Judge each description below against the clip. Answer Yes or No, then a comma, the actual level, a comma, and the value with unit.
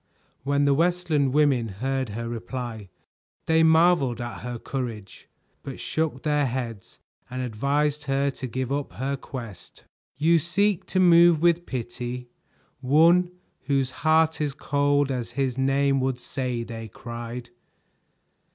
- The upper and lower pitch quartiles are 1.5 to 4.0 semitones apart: Yes, average, 3.7 semitones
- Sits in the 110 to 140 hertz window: Yes, low, 135 Hz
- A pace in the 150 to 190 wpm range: No, slow, 135 wpm